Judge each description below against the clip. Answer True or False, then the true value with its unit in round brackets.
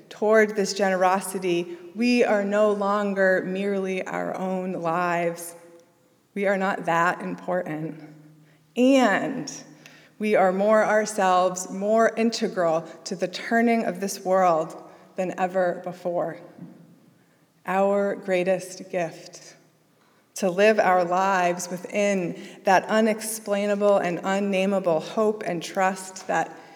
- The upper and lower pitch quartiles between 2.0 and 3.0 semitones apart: True (2.7 semitones)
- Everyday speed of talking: False (110 wpm)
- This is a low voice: False (185 Hz)